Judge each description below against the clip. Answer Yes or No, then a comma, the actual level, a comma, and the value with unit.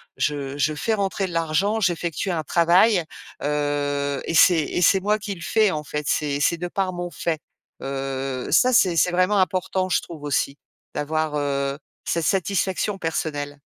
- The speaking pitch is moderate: Yes, medium, 165 Hz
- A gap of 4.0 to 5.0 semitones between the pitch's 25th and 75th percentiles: Yes, average, 4.4 semitones